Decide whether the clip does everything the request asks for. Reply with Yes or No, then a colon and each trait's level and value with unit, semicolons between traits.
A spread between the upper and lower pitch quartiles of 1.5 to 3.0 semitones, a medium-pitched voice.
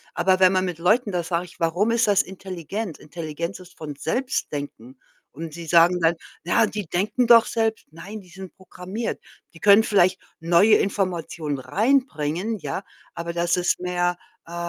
No: average, 3.5 semitones; medium, 180 Hz